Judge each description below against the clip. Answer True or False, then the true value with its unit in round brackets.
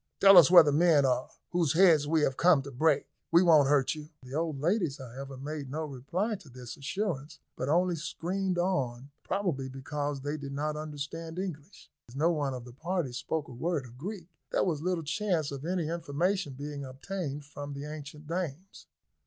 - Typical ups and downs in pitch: True (3.9 semitones)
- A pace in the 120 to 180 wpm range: False (195 wpm)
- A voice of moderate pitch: True (150 Hz)